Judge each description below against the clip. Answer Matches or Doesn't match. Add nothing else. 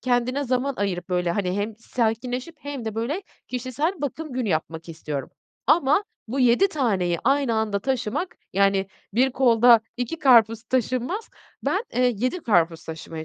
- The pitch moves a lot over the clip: Doesn't match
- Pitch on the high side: Matches